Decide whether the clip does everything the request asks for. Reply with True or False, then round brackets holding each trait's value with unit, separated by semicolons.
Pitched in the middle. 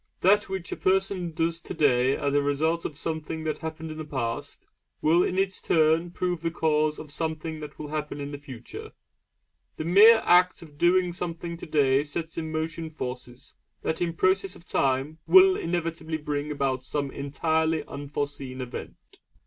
True (160 Hz)